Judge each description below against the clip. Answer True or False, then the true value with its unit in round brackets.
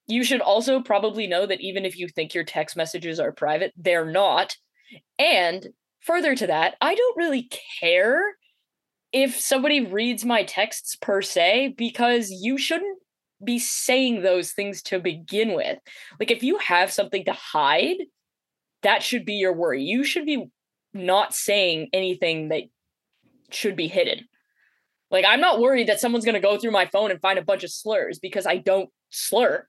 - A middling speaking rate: True (175 wpm)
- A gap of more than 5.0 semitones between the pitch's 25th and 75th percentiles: True (5.6 semitones)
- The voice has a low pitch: False (205 Hz)